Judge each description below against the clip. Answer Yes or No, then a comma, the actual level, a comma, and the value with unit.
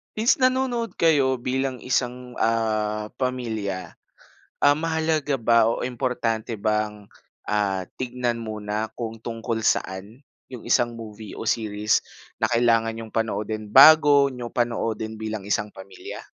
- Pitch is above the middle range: No, low, 115 Hz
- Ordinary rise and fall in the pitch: Yes, average, 3.1 semitones